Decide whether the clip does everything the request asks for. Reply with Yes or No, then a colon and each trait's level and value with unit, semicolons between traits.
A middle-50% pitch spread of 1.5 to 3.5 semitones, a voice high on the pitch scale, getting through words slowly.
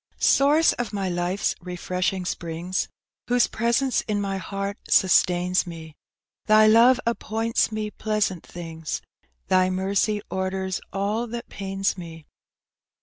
Yes: average, 3.1 semitones; high, 195 Hz; slow, 120 wpm